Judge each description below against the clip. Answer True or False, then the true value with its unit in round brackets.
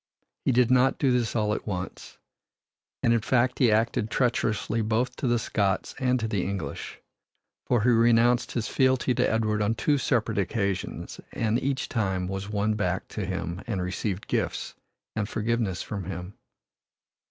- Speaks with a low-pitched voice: True (110 Hz)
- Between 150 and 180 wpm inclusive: True (165 wpm)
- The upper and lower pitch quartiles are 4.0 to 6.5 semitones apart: False (3.4 semitones)